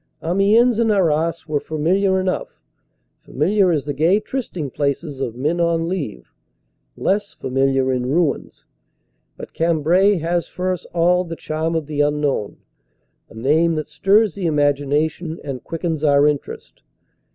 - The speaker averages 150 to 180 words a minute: No, average, 140 wpm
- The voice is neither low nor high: Yes, medium, 160 Hz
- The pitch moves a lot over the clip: No, average, 3.9 semitones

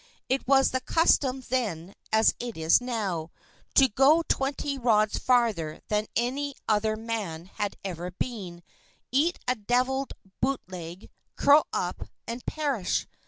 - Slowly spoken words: Yes, slow, 130 wpm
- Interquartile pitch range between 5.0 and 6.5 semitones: Yes, average, 5.3 semitones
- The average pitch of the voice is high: Yes, high, 235 Hz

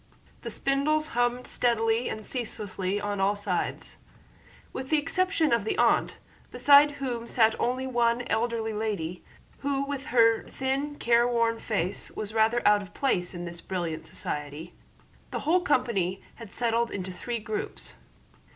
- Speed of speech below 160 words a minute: Yes, average, 145 wpm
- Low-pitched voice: No, high, 230 Hz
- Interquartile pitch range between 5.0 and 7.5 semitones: No, average, 4.3 semitones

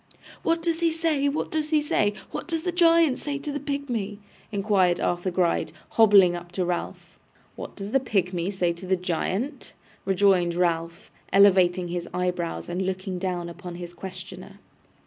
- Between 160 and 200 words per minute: Yes, average, 165 wpm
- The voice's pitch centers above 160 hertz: Yes, high, 190 Hz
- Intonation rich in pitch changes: Yes, wide, 7.9 semitones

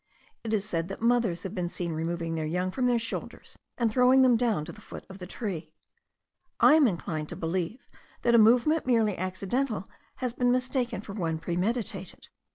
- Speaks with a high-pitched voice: Yes, high, 210 Hz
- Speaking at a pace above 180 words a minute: Yes, average, 190 wpm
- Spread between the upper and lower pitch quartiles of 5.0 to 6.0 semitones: Yes, wide, 5.6 semitones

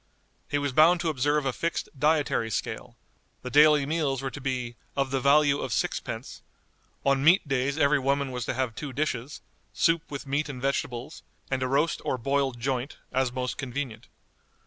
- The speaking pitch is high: No, medium, 140 Hz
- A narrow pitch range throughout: Yes, narrow, 2.3 semitones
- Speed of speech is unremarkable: Yes, average, 180 wpm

